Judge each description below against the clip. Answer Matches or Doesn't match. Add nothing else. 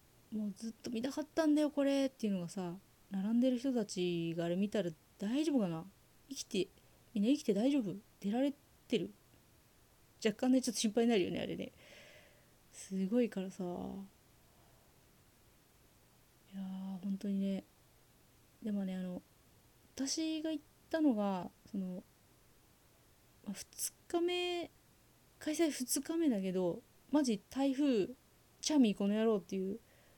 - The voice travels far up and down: Matches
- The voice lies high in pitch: Matches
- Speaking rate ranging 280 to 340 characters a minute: Doesn't match